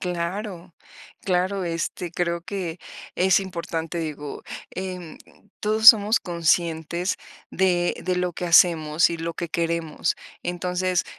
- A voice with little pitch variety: Yes, narrow, 1.6 semitones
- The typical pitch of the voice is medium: Yes, medium, 175 Hz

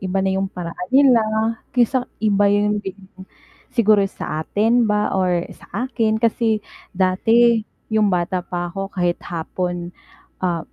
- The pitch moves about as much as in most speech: Yes, average, 3.7 semitones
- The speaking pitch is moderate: No, high, 200 Hz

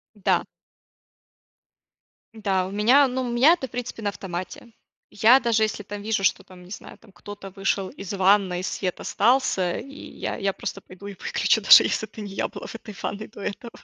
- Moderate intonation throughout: Yes, average, 3.2 semitones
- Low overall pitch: No, high, 205 Hz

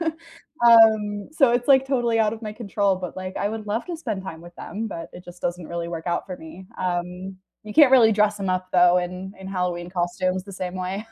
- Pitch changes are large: No, average, 3.7 semitones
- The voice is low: No, high, 190 Hz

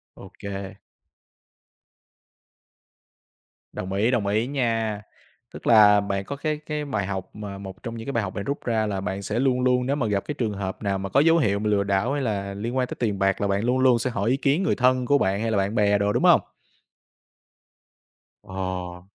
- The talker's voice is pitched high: No, low, 105 Hz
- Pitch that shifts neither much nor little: Yes, average, 4.3 semitones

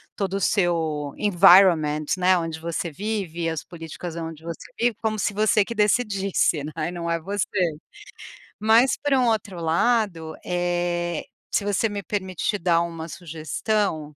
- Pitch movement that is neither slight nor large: Yes, average, 3.9 semitones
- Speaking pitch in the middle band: Yes, medium, 175 Hz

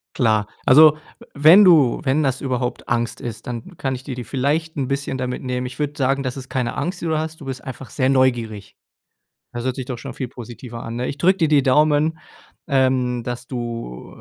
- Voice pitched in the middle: No, low, 130 Hz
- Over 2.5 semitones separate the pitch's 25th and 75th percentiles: Yes, average, 2.9 semitones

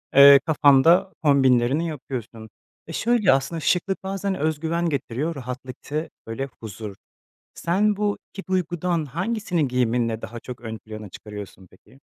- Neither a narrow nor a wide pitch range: No, wide, 6.2 semitones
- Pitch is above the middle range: No, medium, 140 Hz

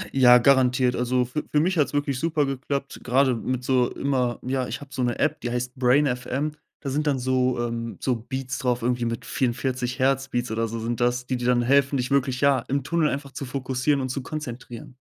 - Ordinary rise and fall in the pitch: No, narrow, 1.9 semitones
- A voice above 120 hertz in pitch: Yes, low, 130 Hz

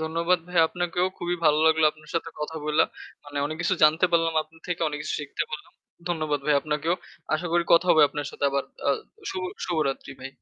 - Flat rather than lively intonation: Yes, narrow, 2.2 semitones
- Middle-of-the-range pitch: Yes, medium, 160 Hz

